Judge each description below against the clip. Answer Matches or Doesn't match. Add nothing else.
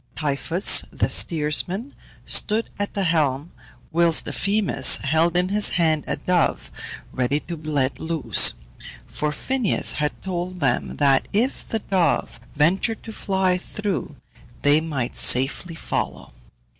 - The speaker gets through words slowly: Matches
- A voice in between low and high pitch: Matches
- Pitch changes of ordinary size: Matches